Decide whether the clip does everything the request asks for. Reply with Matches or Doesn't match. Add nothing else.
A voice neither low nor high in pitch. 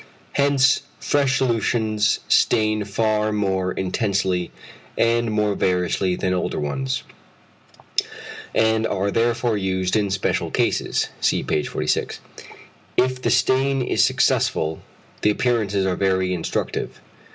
Doesn't match